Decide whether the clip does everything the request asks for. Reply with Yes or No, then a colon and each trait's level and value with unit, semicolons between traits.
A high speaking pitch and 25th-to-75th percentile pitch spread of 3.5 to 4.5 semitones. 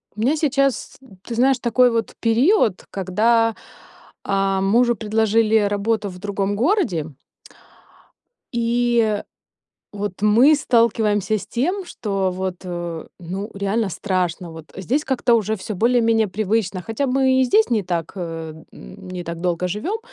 Yes: high, 215 Hz; average, 4.1 semitones